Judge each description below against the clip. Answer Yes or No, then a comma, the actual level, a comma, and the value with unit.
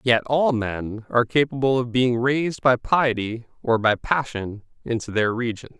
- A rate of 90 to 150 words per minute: No, average, 165 wpm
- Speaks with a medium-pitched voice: No, low, 120 Hz